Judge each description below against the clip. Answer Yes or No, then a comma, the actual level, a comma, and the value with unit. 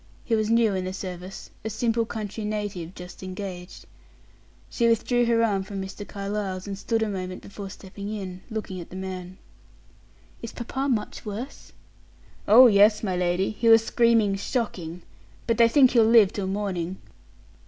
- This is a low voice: No, high, 205 Hz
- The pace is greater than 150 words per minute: Yes, average, 165 wpm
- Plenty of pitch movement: No, average, 3.2 semitones